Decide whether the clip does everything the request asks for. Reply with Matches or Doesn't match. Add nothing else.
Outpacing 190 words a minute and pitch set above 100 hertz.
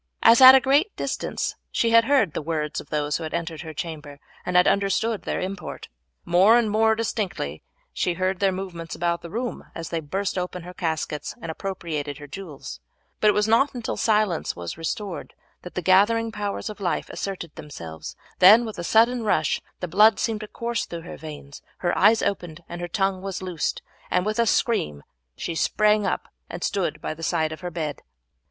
Matches